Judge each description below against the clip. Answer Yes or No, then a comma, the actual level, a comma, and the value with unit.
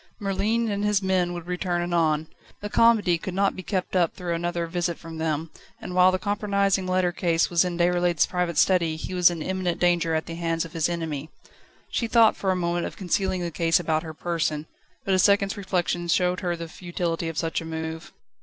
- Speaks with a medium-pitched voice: Yes, medium, 175 Hz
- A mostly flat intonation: Yes, narrow, 2.1 semitones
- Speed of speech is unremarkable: No, fast, 210 wpm